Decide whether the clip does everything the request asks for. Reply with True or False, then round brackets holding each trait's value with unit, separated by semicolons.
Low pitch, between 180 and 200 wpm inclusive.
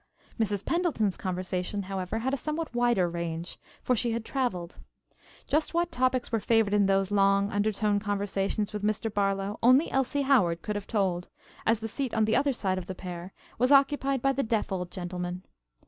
False (210 Hz; 185 wpm)